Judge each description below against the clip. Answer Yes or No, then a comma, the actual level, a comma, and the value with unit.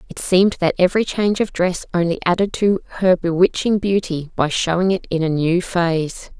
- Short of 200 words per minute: Yes, average, 190 wpm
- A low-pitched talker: No, medium, 180 Hz